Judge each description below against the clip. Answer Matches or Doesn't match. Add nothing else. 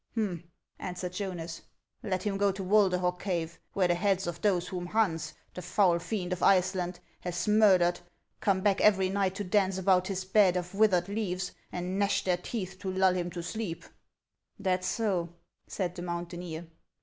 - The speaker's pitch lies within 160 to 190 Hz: Matches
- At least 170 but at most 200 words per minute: Matches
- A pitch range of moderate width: Doesn't match